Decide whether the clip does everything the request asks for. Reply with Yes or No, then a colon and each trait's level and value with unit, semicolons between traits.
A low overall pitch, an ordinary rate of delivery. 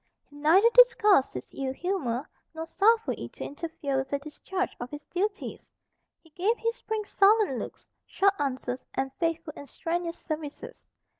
No: very high, 330 Hz; average, 160 wpm